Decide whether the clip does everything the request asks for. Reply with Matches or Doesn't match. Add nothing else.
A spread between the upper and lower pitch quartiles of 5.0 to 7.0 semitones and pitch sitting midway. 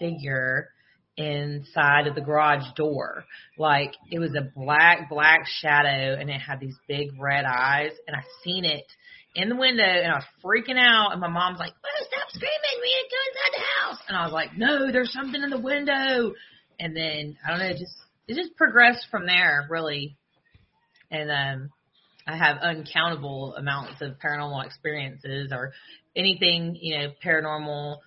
Matches